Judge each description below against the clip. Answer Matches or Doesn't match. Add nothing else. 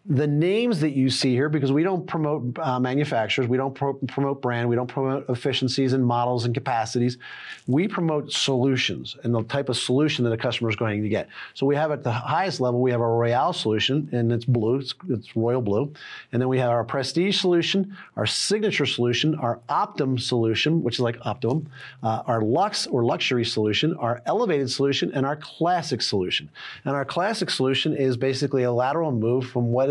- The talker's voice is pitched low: Matches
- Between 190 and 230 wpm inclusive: Matches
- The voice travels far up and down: Doesn't match